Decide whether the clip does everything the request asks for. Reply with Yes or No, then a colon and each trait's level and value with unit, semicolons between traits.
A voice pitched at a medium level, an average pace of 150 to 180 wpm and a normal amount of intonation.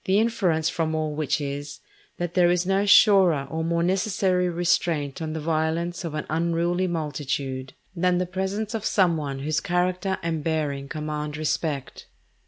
Yes: medium, 165 Hz; average, 165 wpm; average, 3.0 semitones